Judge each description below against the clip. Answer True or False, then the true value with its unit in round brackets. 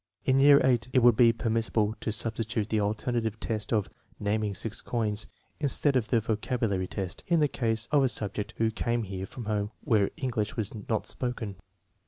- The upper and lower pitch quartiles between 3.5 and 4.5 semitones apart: False (2.5 semitones)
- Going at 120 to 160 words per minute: False (190 wpm)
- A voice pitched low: True (110 Hz)